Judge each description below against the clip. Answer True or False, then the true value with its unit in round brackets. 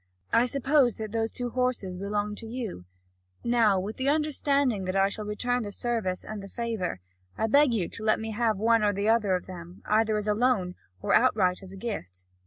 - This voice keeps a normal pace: False (210 wpm)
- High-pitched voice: True (215 Hz)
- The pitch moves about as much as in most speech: True (3.5 semitones)